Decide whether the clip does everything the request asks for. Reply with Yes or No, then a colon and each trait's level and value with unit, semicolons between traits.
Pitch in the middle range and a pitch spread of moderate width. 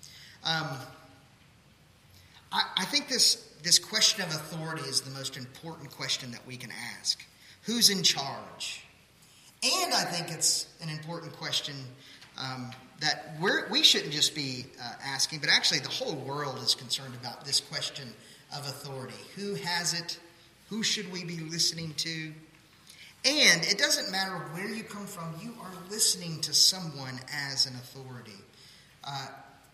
Yes: medium, 155 Hz; average, 4.5 semitones